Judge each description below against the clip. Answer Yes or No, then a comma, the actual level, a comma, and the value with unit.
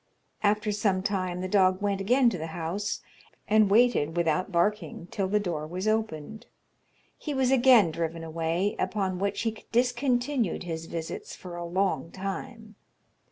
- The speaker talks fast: No, average, 155 wpm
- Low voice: No, high, 195 Hz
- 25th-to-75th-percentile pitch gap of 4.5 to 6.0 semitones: No, average, 4.1 semitones